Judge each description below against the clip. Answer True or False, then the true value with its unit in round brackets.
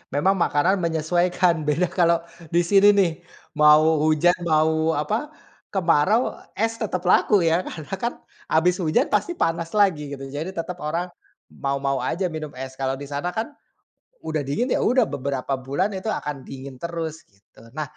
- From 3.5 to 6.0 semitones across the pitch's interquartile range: True (3.8 semitones)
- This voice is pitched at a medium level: True (165 Hz)